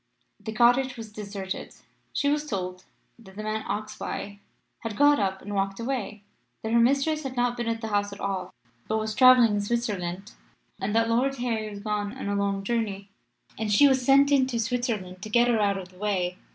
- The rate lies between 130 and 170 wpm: No, fast, 205 wpm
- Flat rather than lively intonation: No, average, 3.3 semitones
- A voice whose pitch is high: Yes, high, 215 Hz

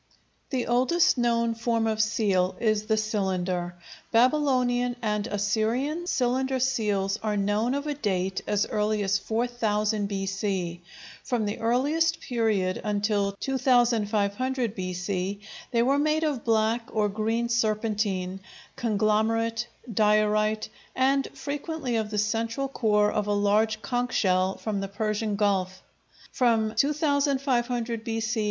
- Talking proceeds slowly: Yes, slow, 125 wpm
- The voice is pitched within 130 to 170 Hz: No, high, 220 Hz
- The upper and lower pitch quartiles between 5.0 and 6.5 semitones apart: No, average, 3.0 semitones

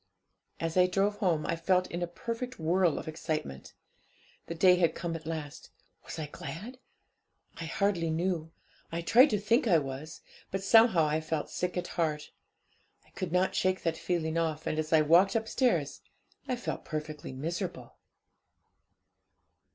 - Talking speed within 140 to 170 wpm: Yes, average, 160 wpm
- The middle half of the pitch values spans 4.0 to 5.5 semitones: No, average, 3.1 semitones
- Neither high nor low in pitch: Yes, medium, 170 Hz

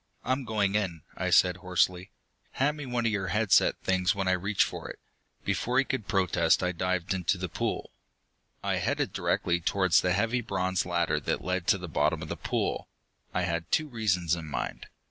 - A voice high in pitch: No, very low, 95 Hz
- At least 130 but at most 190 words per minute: No, average, 200 wpm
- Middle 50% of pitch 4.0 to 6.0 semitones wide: No, average, 3.1 semitones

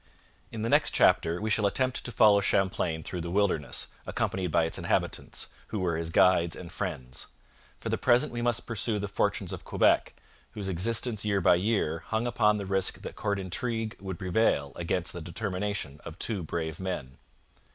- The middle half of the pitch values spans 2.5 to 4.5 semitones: Yes, average, 4.1 semitones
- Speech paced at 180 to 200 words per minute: Yes, average, 185 wpm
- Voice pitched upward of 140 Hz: No, very low, 95 Hz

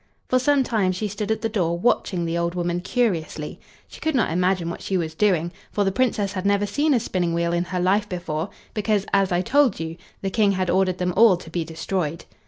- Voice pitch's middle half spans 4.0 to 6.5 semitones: No, average, 3.6 semitones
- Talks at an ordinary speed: No, fast, 230 wpm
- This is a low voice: No, medium, 185 Hz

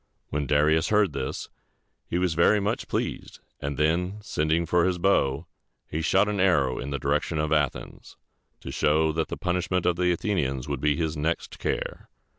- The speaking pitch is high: No, very low, 80 Hz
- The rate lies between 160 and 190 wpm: Yes, average, 180 wpm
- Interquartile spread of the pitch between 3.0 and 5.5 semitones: Yes, average, 3.4 semitones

